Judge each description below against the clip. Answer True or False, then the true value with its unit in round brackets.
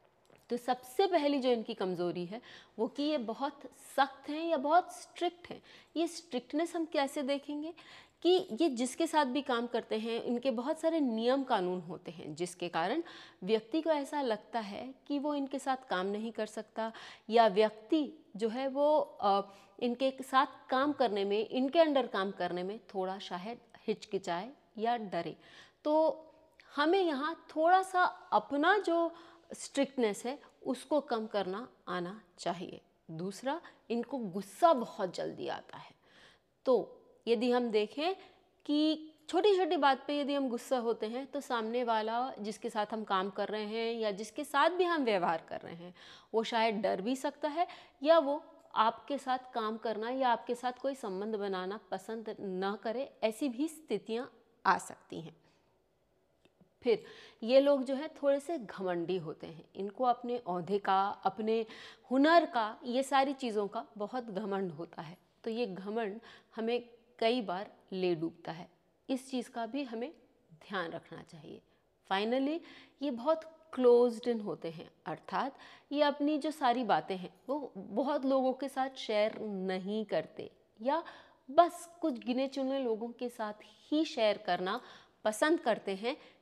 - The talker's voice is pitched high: True (245 Hz)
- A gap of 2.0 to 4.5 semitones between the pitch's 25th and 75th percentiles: False (5.5 semitones)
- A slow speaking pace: False (160 wpm)